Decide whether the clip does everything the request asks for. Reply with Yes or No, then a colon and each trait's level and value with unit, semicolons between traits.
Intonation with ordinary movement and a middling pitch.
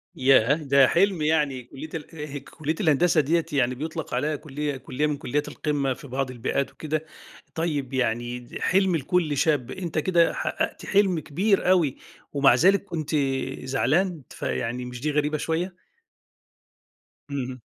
Yes: average, 3.5 semitones; medium, 150 Hz